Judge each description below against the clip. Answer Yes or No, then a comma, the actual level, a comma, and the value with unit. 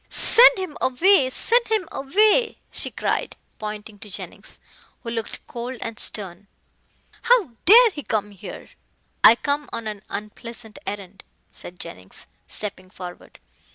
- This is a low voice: No, high, 230 Hz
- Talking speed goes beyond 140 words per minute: No, slow, 135 wpm